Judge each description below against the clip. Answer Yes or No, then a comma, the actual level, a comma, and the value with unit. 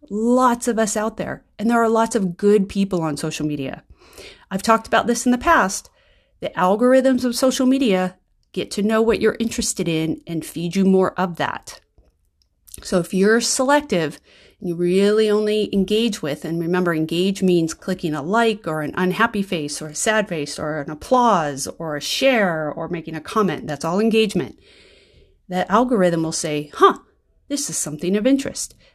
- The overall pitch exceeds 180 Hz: Yes, high, 190 Hz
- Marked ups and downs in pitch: Yes, wide, 5.7 semitones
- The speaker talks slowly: No, average, 180 wpm